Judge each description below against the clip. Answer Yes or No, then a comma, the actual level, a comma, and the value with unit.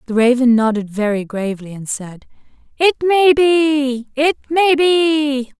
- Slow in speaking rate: Yes, slow, 130 wpm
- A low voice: No, very high, 270 Hz